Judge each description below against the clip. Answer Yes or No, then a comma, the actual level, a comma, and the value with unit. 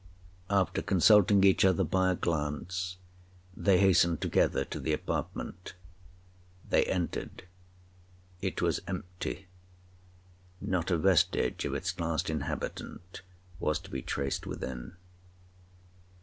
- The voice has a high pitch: No, very low, 90 Hz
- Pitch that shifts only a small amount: Yes, narrow, 1.2 semitones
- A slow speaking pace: Yes, slow, 105 wpm